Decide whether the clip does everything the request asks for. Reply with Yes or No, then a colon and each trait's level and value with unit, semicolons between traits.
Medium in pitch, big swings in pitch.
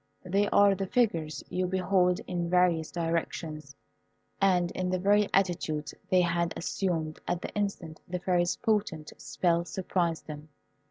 No: medium, 180 Hz; narrow, 2.4 semitones